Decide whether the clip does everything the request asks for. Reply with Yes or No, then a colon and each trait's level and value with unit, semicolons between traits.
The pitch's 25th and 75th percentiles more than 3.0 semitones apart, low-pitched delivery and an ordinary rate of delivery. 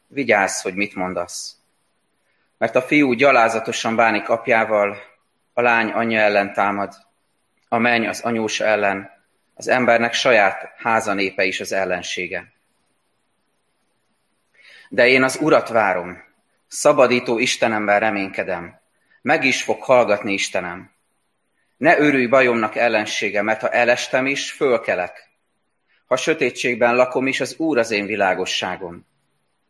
Yes: average, 3.5 semitones; low, 110 Hz; average, 120 wpm